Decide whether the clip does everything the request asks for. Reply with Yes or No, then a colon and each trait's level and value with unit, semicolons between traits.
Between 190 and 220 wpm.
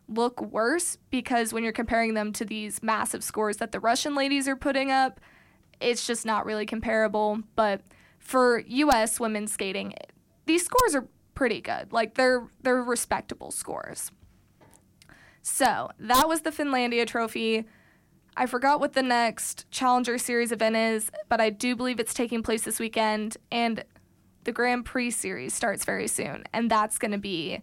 No: average, 165 wpm